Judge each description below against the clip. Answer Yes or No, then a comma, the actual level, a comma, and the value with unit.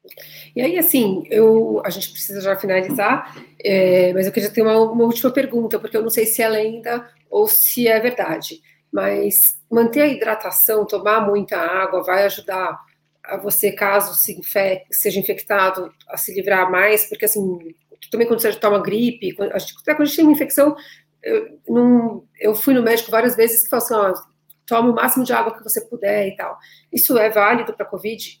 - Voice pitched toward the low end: No, high, 215 Hz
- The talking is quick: Yes, fast, 190 wpm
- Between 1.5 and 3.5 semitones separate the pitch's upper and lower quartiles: Yes, average, 2.9 semitones